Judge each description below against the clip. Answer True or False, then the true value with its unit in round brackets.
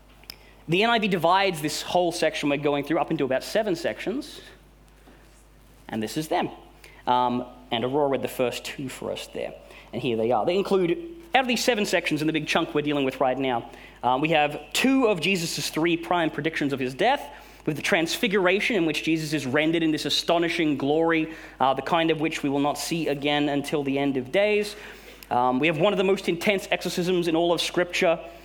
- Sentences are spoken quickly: True (210 wpm)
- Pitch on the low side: False (160 Hz)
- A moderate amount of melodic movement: True (4.1 semitones)